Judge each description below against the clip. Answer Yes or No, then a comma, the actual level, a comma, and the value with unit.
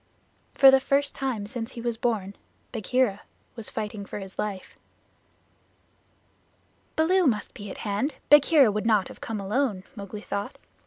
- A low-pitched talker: No, high, 225 Hz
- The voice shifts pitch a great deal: No, average, 4.7 semitones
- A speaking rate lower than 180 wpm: Yes, average, 150 wpm